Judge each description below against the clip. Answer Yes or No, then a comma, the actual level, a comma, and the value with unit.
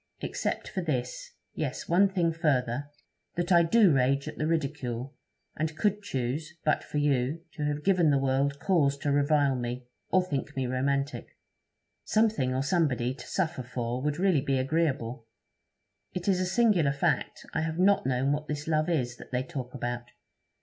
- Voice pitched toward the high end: No, medium, 145 Hz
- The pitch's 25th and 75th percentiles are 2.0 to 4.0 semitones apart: No, average, 4.4 semitones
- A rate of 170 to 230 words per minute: Yes, average, 175 wpm